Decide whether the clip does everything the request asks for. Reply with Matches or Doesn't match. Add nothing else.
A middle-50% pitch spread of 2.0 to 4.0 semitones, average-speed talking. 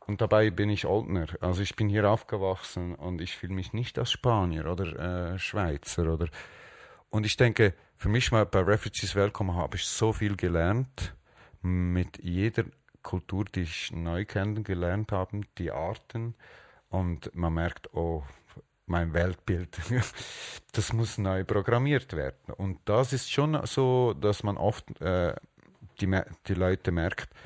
Matches